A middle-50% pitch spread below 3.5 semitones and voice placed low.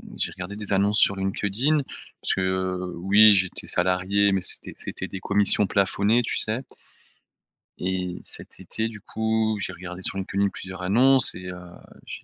Yes: narrow, 2.5 semitones; low, 100 Hz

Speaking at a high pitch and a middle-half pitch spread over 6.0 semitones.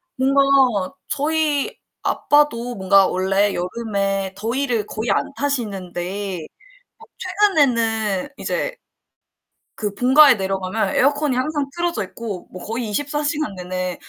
Yes: high, 230 Hz; wide, 6.6 semitones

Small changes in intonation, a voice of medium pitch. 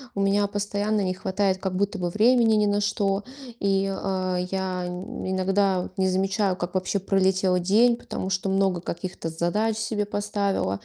No: narrow, 1.7 semitones; high, 195 Hz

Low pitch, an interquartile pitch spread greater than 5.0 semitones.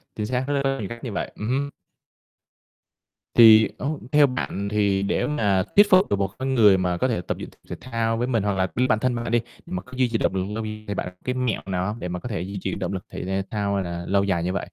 No: low, 110 Hz; average, 4.6 semitones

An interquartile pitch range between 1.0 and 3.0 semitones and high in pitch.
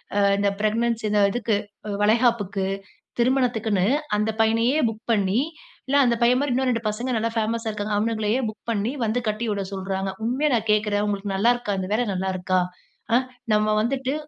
Yes: narrow, 2.5 semitones; high, 220 Hz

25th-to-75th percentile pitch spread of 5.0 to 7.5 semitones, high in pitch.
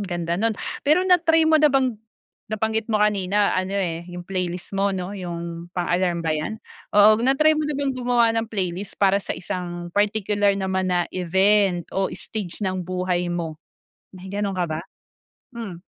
No: average, 3.6 semitones; high, 195 Hz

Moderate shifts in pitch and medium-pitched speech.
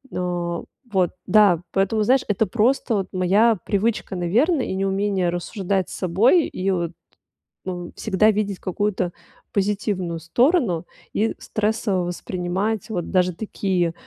No: average, 3.2 semitones; high, 195 Hz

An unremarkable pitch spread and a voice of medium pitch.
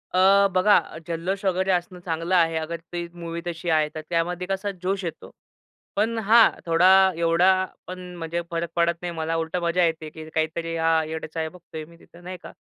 No: narrow, 1.9 semitones; medium, 170 Hz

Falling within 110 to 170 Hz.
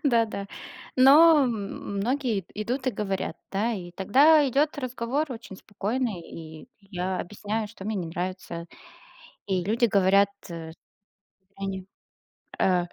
No: high, 205 Hz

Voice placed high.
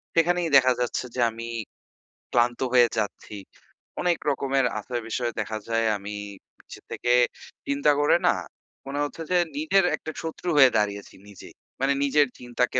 No: low, 130 Hz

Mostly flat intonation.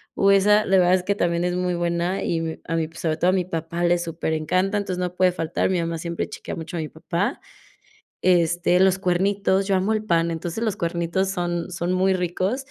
Yes: narrow, 2.1 semitones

